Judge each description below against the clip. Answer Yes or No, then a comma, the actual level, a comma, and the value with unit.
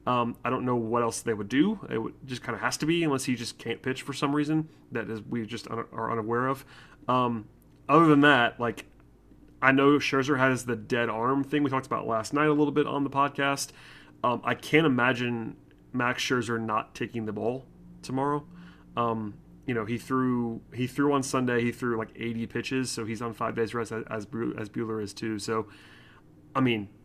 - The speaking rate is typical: No, fast, 215 wpm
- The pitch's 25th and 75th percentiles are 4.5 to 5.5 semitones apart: No, average, 3.4 semitones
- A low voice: Yes, low, 120 Hz